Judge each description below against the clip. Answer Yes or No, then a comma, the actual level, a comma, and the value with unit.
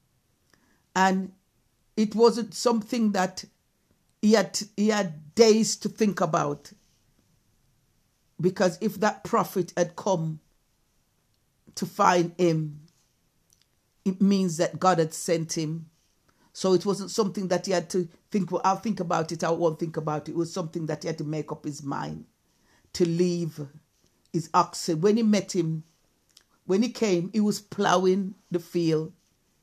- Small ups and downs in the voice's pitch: No, average, 3.7 semitones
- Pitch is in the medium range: Yes, medium, 180 Hz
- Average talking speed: Yes, average, 150 wpm